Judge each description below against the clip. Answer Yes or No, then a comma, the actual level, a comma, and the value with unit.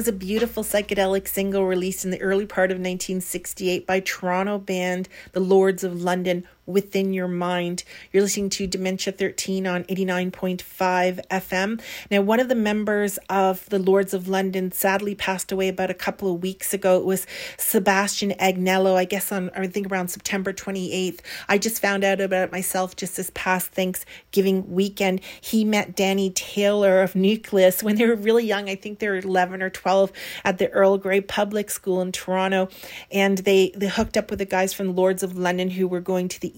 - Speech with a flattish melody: Yes, narrow, 1.2 semitones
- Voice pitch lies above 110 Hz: Yes, high, 190 Hz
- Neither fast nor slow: Yes, average, 195 wpm